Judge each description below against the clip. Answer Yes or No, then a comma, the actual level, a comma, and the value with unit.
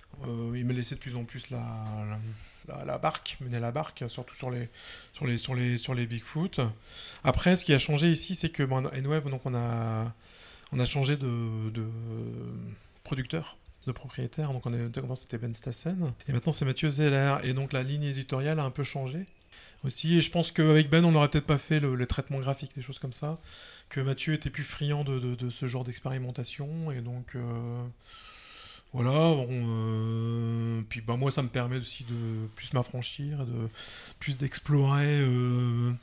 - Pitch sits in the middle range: No, low, 130 Hz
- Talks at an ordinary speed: Yes, average, 195 wpm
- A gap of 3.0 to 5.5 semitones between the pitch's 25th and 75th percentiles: Yes, average, 3.3 semitones